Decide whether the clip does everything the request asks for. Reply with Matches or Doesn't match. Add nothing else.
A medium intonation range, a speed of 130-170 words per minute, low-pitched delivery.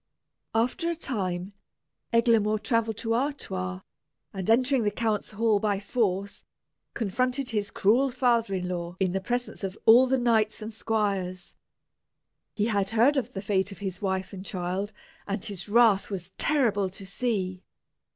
Doesn't match